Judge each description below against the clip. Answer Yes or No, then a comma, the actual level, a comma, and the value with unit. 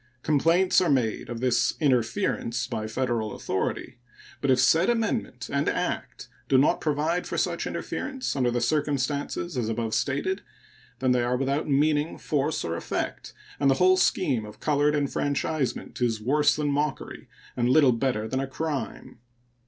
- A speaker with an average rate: Yes, average, 160 wpm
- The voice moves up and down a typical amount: Yes, average, 3.8 semitones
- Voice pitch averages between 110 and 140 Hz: Yes, low, 135 Hz